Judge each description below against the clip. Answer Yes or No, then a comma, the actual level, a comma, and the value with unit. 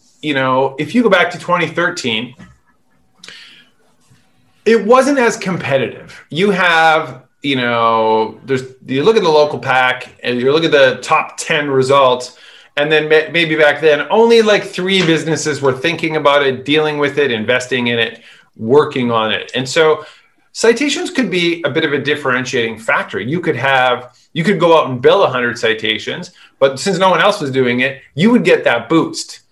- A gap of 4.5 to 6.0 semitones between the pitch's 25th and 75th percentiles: Yes, average, 5.2 semitones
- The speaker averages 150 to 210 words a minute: Yes, average, 180 wpm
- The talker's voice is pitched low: No, medium, 150 Hz